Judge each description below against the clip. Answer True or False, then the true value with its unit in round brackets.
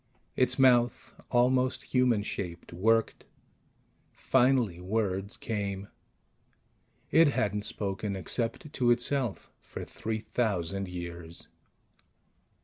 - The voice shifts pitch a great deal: False (4.2 semitones)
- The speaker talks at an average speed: False (90 wpm)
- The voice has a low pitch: True (110 Hz)